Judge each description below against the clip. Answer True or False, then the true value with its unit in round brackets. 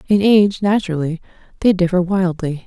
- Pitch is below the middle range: False (185 Hz)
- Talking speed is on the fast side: False (135 wpm)